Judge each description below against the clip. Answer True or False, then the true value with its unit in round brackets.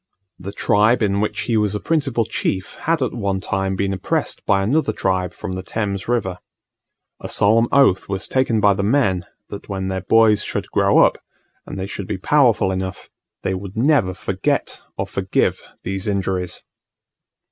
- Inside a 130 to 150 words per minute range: False (175 wpm)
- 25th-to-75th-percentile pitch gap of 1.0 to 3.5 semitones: True (3.1 semitones)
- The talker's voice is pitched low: True (100 Hz)